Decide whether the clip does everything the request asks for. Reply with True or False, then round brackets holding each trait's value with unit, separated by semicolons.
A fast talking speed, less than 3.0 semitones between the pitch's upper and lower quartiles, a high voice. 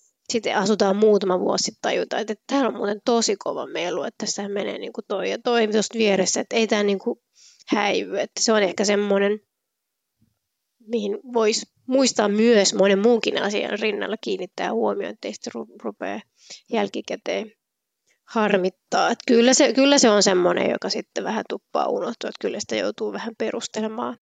True (160 wpm; 2.5 semitones; 220 Hz)